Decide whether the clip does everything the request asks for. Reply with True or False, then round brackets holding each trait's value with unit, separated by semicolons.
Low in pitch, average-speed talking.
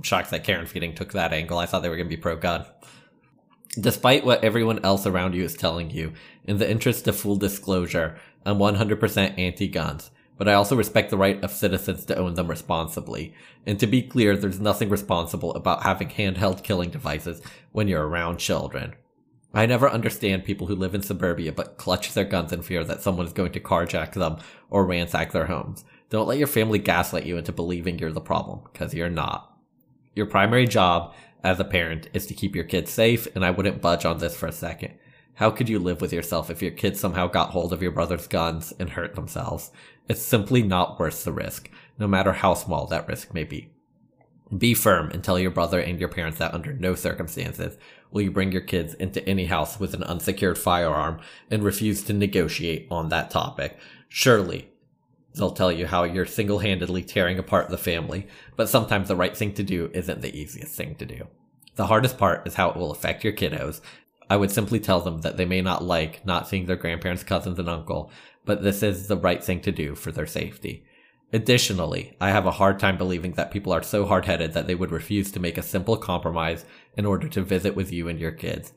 False (95 Hz; 210 wpm)